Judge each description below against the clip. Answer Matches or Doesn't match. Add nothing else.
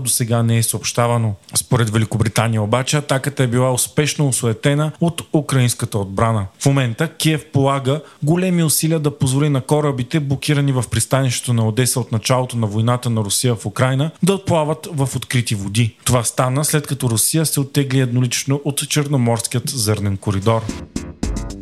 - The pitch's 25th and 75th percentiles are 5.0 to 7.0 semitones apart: Doesn't match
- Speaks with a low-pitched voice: Matches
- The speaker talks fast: Doesn't match